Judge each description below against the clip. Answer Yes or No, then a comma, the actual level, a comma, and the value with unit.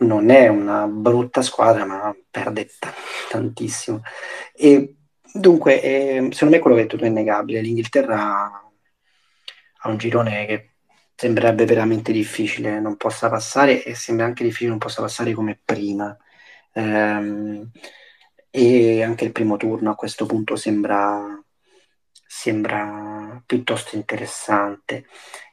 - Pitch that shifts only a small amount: Yes, narrow, 2.1 semitones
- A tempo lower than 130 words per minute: Yes, average, 120 wpm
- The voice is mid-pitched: No, low, 110 Hz